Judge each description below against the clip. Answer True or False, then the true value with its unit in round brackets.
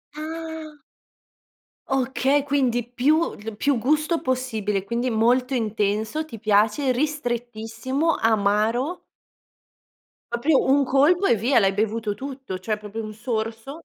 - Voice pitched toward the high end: True (245 Hz)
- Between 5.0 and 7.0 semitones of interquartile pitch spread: False (4.5 semitones)